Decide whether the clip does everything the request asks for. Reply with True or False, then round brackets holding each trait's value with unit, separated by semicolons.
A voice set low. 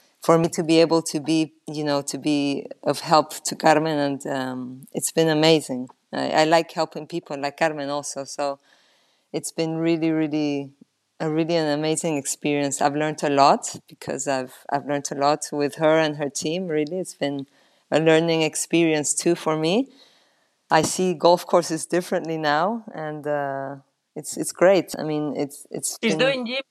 False (155 Hz)